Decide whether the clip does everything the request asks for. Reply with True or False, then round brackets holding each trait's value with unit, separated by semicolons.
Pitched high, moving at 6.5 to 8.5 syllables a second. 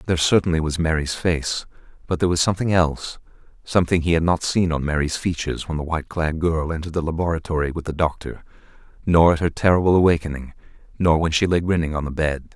False (80 Hz; 6.6 syllables/s)